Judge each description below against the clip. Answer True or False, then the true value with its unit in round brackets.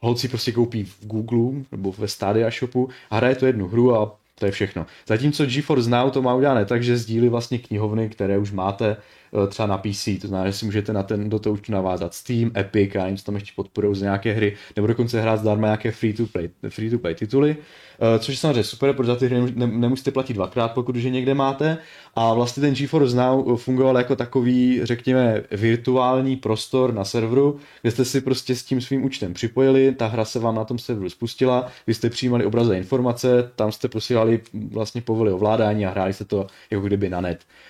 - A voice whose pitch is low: True (115 Hz)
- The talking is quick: True (205 wpm)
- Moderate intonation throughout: True (3.3 semitones)